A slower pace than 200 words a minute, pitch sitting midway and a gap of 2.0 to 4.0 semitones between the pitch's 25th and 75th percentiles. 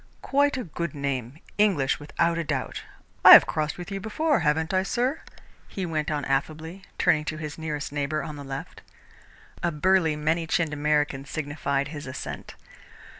Yes: average, 170 wpm; medium, 155 Hz; average, 3.0 semitones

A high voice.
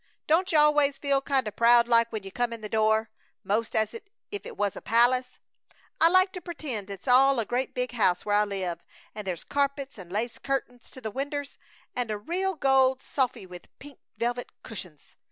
Yes: high, 245 Hz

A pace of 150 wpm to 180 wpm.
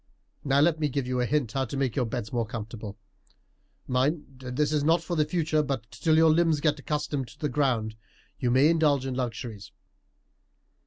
No: average, 190 wpm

